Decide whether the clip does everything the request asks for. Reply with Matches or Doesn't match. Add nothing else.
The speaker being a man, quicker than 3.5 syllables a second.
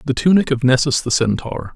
Matches